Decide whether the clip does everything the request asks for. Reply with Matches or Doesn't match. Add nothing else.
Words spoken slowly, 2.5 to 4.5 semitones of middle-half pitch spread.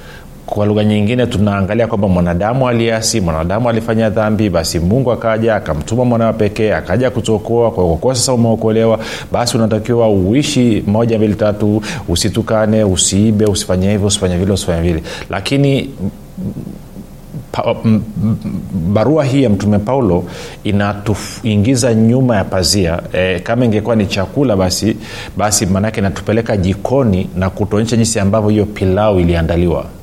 Doesn't match